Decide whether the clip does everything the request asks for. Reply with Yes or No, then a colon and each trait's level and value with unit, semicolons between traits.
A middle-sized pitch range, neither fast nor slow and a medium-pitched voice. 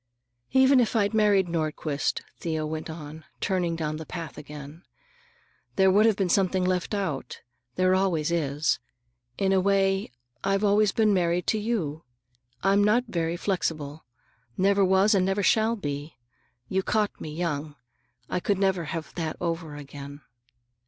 Yes: average, 4.1 semitones; average, 150 wpm; medium, 180 Hz